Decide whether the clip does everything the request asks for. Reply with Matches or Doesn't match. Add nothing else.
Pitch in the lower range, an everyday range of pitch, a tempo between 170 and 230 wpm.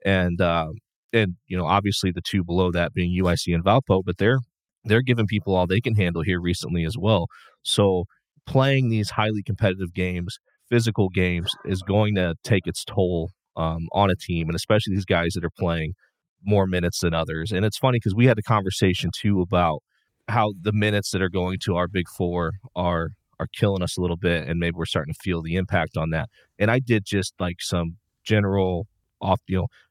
Matches